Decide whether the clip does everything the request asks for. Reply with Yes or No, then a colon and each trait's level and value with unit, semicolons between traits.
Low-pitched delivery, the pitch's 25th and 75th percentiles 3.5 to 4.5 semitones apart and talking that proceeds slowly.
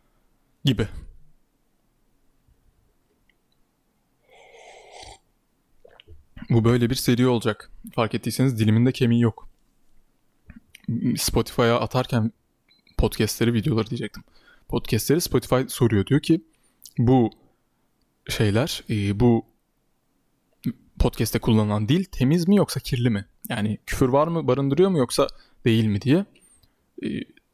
No: low, 120 Hz; average, 3.0 semitones; slow, 90 wpm